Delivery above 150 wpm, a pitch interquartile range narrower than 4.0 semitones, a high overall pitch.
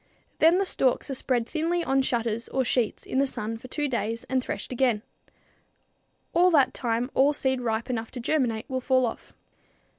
Yes: average, 185 wpm; average, 2.8 semitones; very high, 255 Hz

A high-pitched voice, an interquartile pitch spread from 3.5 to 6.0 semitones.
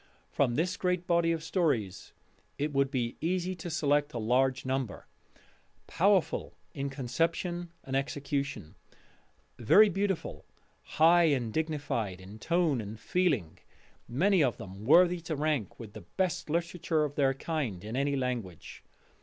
No: medium, 145 Hz; wide, 5.5 semitones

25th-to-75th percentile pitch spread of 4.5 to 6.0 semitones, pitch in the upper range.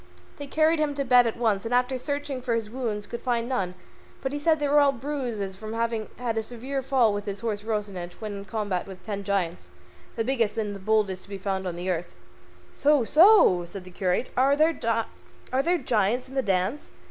Yes: average, 5.0 semitones; high, 230 Hz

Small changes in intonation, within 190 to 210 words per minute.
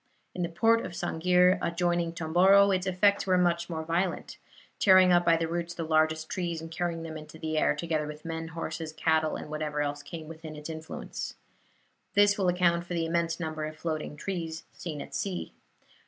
Yes: narrow, 2.0 semitones; average, 195 wpm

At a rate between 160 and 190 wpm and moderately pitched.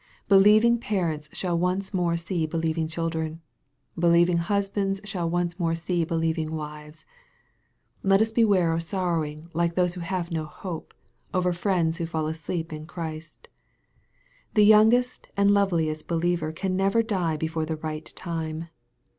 No: average, 145 wpm; medium, 170 Hz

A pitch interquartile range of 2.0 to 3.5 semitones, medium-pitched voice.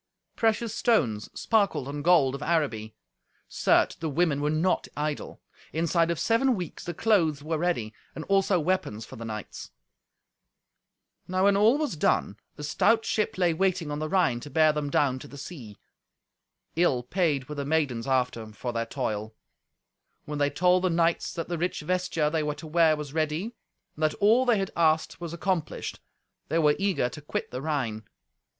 No: average, 4.2 semitones; medium, 155 Hz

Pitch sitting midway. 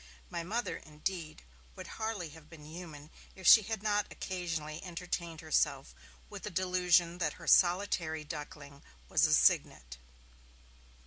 Yes: medium, 170 Hz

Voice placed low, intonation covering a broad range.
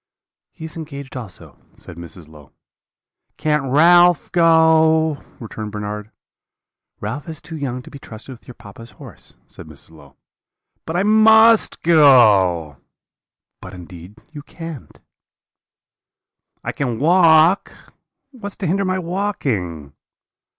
No: medium, 145 Hz; wide, 8.0 semitones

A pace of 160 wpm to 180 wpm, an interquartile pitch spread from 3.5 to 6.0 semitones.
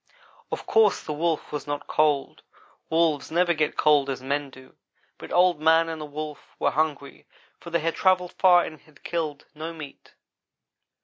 No: average, 175 wpm; narrow, 2.5 semitones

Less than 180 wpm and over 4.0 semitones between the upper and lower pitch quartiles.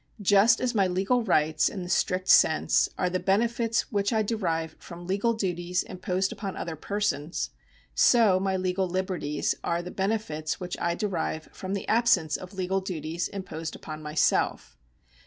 No: average, 160 wpm; average, 2.9 semitones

